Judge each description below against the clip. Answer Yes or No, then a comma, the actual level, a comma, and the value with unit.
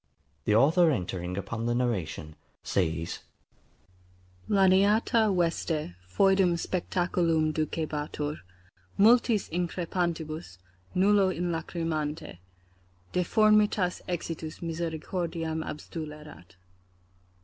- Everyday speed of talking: No, slow, 70 wpm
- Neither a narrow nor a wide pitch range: Yes, average, 3.5 semitones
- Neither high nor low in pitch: Yes, medium, 165 Hz